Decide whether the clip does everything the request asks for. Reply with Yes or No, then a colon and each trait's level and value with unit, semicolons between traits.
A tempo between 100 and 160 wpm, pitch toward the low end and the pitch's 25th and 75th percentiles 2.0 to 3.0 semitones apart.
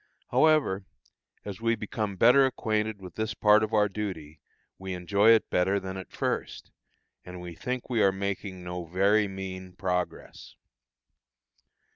Yes: average, 145 wpm; low, 100 Hz; average, 2.7 semitones